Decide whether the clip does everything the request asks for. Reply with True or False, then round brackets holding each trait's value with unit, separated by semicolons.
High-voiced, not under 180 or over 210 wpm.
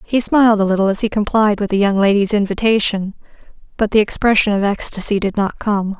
True (205 Hz; 200 wpm)